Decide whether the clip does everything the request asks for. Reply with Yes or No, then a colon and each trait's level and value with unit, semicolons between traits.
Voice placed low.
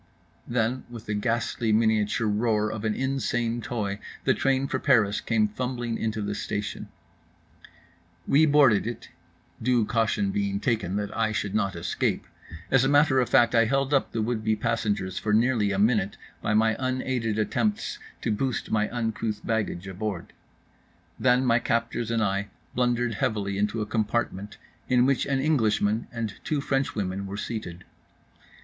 Yes: low, 115 Hz